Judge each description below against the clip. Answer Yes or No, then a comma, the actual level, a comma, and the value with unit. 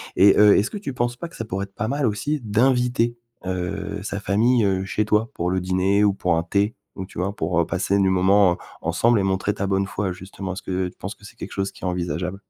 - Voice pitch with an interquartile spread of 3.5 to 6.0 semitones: No, narrow, 2.6 semitones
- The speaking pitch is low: Yes, low, 100 Hz